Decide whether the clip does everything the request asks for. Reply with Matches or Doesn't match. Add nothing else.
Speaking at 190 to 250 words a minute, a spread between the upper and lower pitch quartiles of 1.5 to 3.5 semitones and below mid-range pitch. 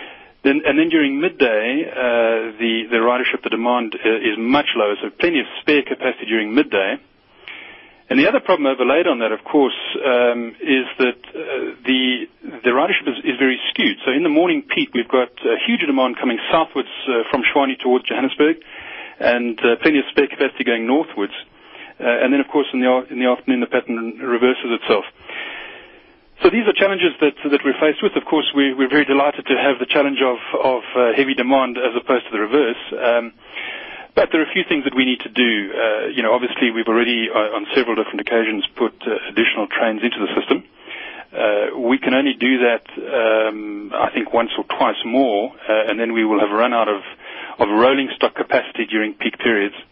Doesn't match